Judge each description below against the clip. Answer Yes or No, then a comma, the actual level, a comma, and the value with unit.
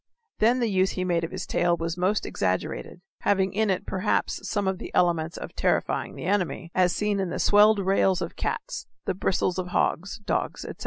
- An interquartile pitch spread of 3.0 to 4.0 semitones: No, narrow, 2.6 semitones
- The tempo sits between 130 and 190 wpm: No, fast, 205 wpm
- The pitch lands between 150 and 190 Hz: Yes, medium, 185 Hz